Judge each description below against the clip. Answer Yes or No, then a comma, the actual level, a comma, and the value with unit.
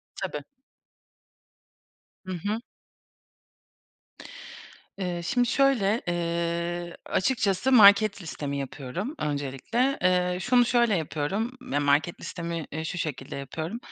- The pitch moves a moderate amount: No, wide, 5.8 semitones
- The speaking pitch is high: No, medium, 180 Hz